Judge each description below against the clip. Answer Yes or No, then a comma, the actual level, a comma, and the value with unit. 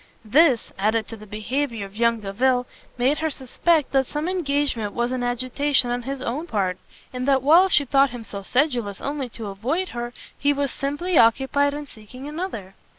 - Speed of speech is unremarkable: Yes, average, 185 wpm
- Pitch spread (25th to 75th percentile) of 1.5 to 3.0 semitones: No, average, 4.0 semitones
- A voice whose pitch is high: Yes, very high, 255 Hz